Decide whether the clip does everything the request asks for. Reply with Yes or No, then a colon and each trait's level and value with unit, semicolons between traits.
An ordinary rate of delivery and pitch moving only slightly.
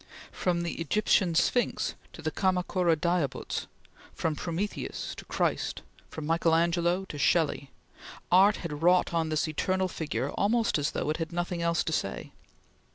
Yes: average, 155 wpm; narrow, 2.2 semitones